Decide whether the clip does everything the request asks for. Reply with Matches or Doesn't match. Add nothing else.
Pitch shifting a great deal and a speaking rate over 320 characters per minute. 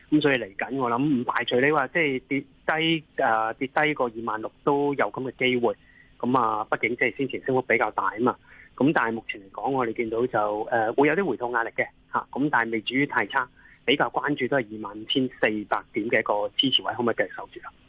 Doesn't match